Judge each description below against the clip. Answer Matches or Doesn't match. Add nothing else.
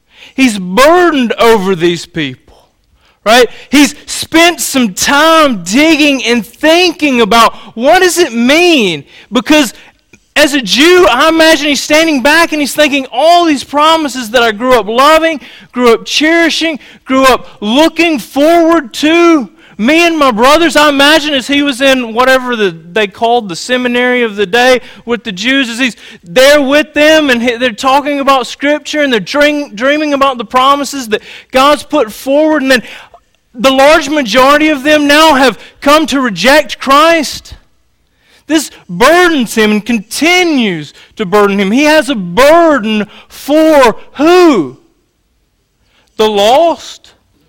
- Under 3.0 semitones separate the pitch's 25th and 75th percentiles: Doesn't match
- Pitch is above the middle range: Matches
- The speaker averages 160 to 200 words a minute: Doesn't match